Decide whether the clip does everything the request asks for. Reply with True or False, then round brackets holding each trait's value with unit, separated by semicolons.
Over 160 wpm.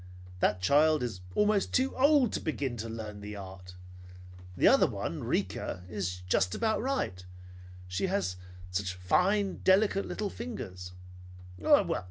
False (140 wpm)